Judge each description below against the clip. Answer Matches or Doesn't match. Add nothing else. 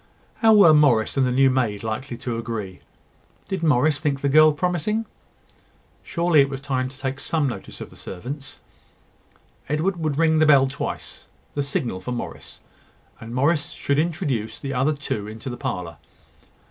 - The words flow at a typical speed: Matches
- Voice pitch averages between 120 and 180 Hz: Matches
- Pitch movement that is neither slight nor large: Matches